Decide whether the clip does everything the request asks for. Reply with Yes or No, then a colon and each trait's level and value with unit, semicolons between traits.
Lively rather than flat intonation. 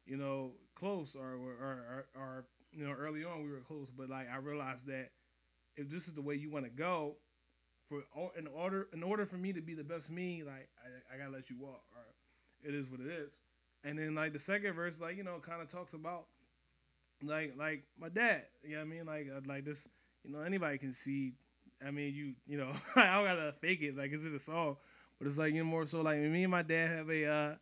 No: average, 3.5 semitones